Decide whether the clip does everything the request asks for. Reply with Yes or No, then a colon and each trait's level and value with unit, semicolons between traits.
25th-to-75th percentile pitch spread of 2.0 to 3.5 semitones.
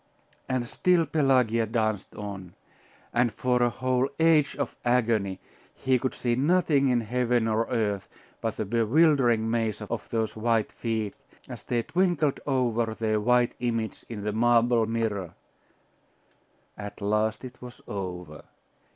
Yes: average, 2.7 semitones